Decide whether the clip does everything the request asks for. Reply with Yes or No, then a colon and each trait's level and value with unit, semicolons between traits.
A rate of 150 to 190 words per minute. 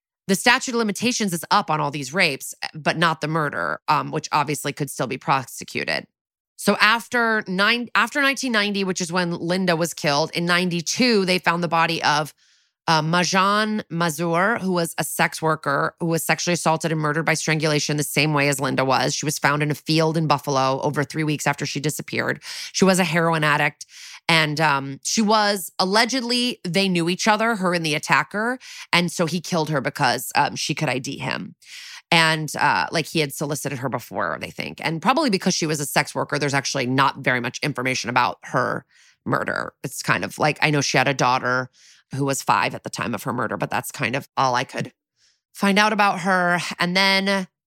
No: fast, 205 wpm